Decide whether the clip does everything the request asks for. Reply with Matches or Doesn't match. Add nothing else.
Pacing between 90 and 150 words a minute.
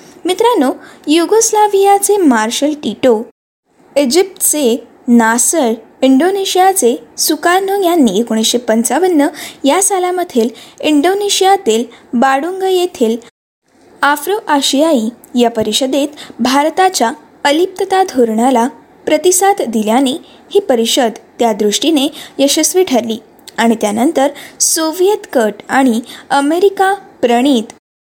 Doesn't match